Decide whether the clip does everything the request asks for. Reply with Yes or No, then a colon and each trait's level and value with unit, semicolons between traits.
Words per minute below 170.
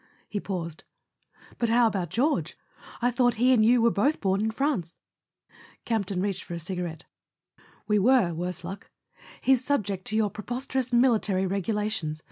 Yes: average, 160 wpm